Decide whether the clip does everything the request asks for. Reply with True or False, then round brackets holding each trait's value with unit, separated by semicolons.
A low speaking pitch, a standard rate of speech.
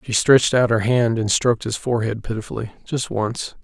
True (115 Hz; 180 wpm)